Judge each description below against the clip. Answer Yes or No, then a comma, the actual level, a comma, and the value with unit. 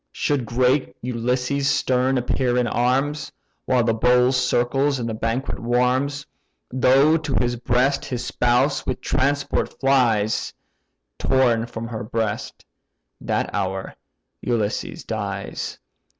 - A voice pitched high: No, low, 125 Hz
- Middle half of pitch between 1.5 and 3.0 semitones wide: Yes, narrow, 2.4 semitones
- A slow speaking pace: Yes, slow, 120 wpm